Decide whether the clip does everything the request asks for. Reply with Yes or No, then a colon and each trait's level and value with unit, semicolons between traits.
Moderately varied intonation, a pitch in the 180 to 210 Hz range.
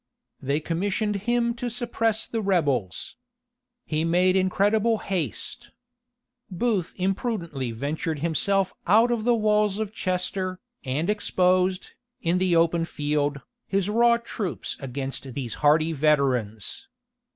No: wide, 5.8 semitones; medium, 185 Hz